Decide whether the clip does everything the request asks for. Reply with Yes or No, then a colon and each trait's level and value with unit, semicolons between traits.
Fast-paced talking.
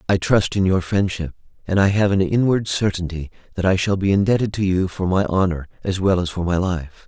Yes: fast, 230 wpm